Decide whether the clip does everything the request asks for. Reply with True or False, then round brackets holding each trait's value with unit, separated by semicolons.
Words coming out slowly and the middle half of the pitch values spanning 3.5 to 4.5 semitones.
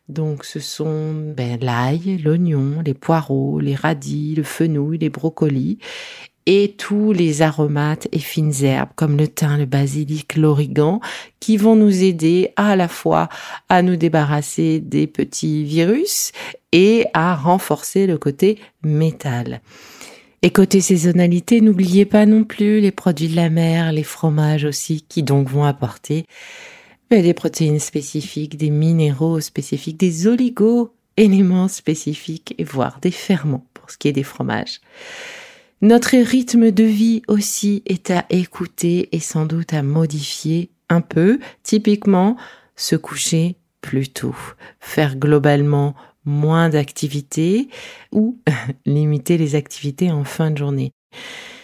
False (140 wpm; 5.0 semitones)